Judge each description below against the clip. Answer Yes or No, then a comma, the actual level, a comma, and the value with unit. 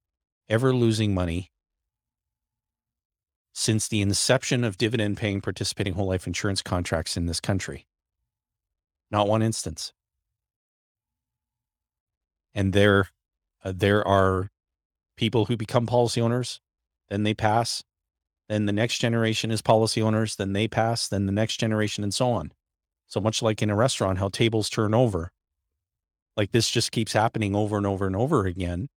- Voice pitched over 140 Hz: No, low, 100 Hz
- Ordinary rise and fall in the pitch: Yes, average, 4.0 semitones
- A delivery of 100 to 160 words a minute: Yes, average, 145 wpm